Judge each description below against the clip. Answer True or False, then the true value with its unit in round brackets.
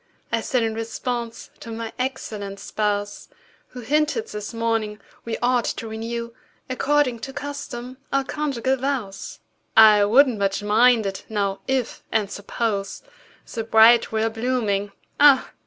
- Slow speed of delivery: True (130 wpm)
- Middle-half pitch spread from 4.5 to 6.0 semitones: False (3.3 semitones)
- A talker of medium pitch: False (230 Hz)